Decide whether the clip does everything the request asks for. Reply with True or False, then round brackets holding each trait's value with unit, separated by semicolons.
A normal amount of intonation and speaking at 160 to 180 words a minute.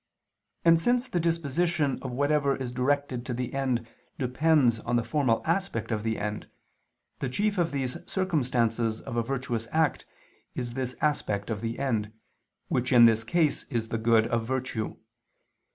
True (4.4 semitones; 165 wpm)